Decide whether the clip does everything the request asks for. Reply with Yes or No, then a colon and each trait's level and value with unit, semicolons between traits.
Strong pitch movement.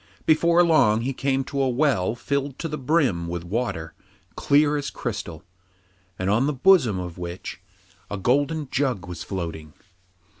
Yes: wide, 7.7 semitones